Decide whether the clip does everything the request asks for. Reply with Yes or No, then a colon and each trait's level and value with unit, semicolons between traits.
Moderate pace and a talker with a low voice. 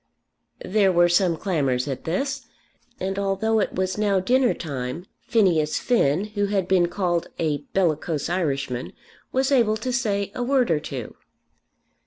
No: average, 150 wpm; high, 190 Hz